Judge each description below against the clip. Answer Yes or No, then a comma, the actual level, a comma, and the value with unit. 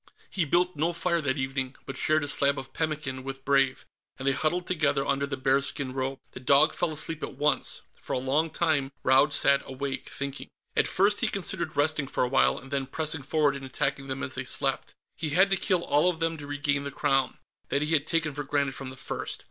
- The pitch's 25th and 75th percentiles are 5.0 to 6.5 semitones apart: No, average, 2.7 semitones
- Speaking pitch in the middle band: Yes, medium, 145 Hz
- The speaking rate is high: Yes, fast, 230 wpm